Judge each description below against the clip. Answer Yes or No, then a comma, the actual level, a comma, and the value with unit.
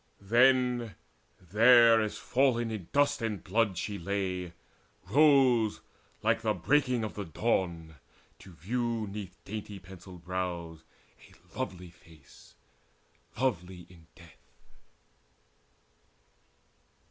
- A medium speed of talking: No, slow, 100 wpm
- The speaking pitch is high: No, low, 100 Hz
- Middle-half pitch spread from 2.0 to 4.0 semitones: No, average, 4.9 semitones